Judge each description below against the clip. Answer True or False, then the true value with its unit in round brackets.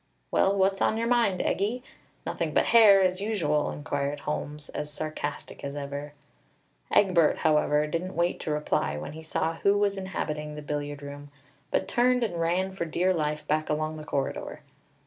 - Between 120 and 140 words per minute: False (170 wpm)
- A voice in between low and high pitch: True (160 Hz)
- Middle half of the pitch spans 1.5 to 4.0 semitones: False (4.5 semitones)